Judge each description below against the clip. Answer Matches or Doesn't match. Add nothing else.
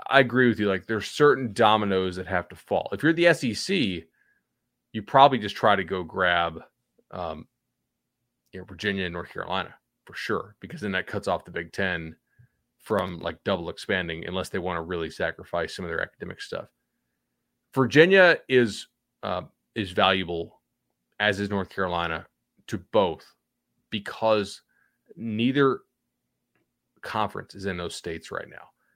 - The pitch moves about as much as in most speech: Doesn't match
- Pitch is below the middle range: Matches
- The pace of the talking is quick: Doesn't match